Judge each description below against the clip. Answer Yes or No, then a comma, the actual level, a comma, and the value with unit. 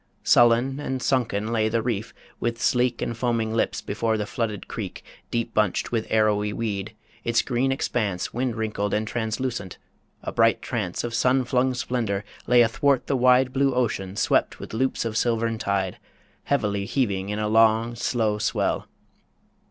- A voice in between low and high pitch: No, low, 115 Hz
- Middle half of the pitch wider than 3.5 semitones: No, narrow, 2.6 semitones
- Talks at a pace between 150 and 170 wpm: Yes, average, 160 wpm